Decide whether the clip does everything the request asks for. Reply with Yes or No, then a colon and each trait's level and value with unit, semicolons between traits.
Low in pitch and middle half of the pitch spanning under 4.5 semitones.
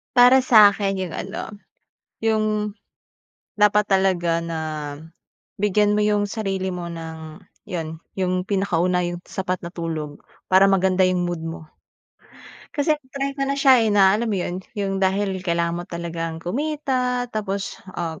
No: high, 190 Hz; average, 3.4 semitones